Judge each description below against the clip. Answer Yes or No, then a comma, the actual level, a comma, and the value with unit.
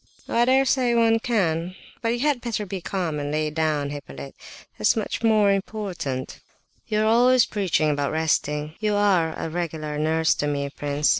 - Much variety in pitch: Yes, wide, 6.6 semitones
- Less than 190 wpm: Yes, average, 175 wpm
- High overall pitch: No, medium, 175 Hz